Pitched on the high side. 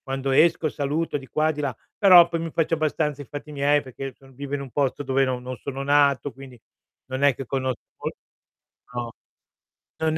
No: medium, 140 Hz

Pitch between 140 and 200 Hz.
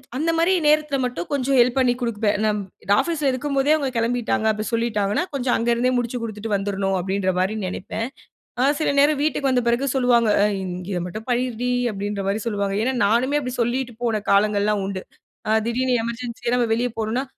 No: high, 235 Hz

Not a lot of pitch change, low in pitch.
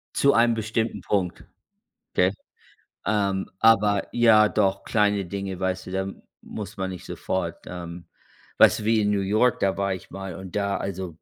Yes: narrow, 2.1 semitones; low, 100 Hz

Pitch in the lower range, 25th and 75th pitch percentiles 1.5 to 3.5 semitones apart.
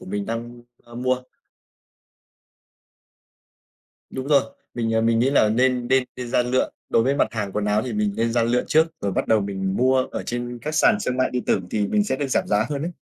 Yes: low, 120 Hz; average, 2.9 semitones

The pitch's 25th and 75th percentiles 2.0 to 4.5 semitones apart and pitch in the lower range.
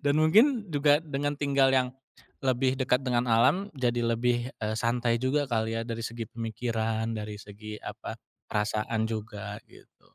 Yes: average, 3.5 semitones; low, 120 Hz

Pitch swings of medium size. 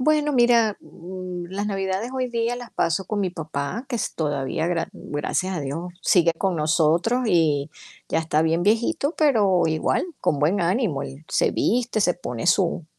No: wide, 6.0 semitones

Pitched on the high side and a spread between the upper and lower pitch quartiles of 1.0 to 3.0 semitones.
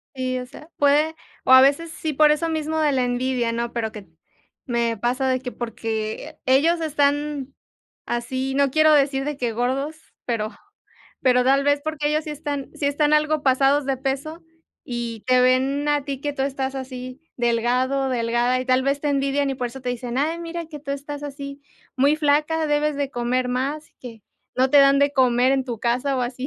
Yes: very high, 270 Hz; average, 2.7 semitones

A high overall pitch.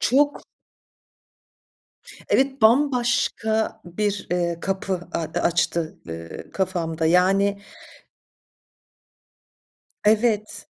Yes: high, 195 Hz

